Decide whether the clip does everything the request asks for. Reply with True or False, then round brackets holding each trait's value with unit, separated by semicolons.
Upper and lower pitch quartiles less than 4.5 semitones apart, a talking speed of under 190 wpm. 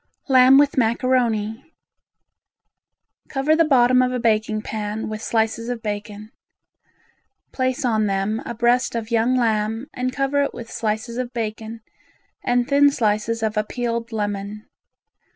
True (2.8 semitones; 140 wpm)